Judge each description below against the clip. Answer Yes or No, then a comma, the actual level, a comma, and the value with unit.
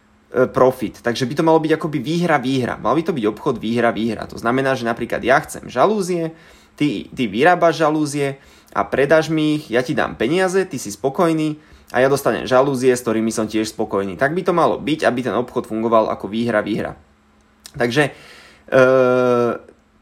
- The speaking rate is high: Yes, fast, 185 wpm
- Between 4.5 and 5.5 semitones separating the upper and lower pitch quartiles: Yes, average, 5.0 semitones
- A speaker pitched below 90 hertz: No, low, 130 Hz